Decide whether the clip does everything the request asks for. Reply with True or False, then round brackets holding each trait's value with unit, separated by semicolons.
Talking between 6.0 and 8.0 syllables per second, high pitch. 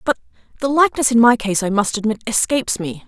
True (6.3 syllables/s; 230 Hz)